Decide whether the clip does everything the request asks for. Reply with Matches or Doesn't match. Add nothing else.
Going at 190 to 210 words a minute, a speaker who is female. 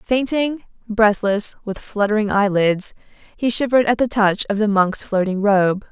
Doesn't match